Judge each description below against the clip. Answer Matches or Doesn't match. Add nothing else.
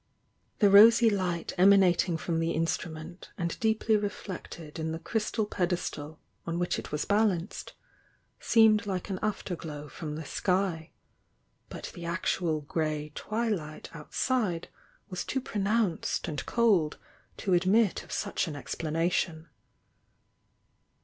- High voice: Doesn't match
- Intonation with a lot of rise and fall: Doesn't match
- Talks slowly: Matches